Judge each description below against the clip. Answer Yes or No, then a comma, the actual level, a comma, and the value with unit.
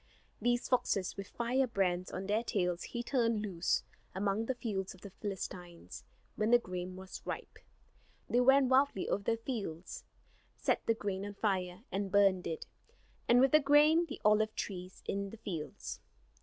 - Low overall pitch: No, high, 205 Hz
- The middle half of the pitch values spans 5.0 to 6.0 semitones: No, average, 4.3 semitones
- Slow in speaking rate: No, average, 165 wpm